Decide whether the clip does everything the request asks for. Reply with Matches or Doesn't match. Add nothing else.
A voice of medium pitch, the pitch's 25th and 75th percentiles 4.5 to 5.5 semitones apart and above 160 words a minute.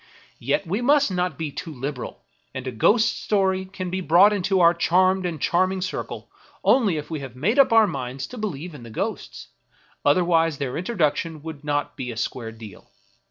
Matches